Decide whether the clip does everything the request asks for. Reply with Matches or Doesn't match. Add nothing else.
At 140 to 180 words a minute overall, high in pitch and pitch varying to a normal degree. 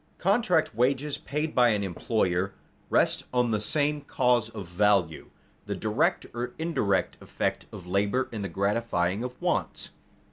Doesn't match